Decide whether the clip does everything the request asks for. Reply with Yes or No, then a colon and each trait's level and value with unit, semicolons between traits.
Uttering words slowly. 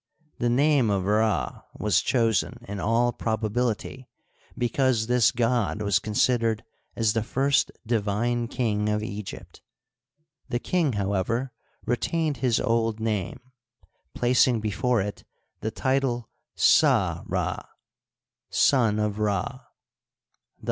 Yes: slow, 115 wpm